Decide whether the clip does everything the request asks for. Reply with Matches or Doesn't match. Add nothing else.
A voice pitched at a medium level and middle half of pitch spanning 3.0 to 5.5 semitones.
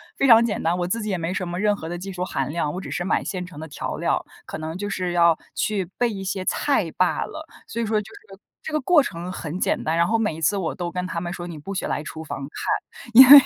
Matches